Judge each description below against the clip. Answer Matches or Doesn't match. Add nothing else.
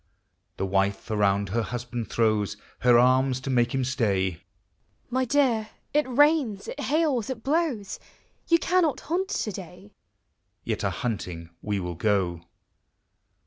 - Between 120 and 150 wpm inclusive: Matches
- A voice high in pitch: Doesn't match